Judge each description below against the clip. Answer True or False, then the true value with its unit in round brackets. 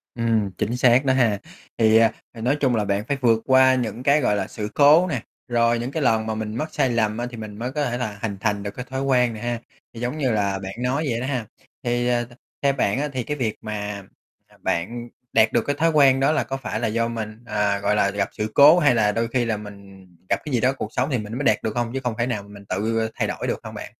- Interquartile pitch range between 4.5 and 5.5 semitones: False (3.4 semitones)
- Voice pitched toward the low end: True (115 Hz)